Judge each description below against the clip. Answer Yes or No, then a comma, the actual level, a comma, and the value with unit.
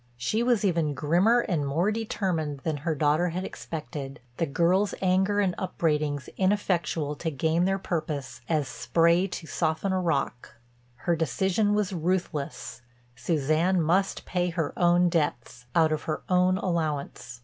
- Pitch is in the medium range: Yes, medium, 170 Hz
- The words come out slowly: No, average, 150 wpm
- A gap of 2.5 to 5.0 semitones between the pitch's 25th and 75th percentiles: Yes, average, 3.7 semitones